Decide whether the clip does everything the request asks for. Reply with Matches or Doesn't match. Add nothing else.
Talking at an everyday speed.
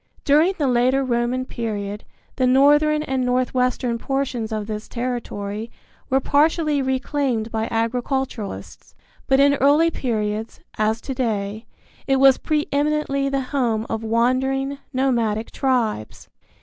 Doesn't match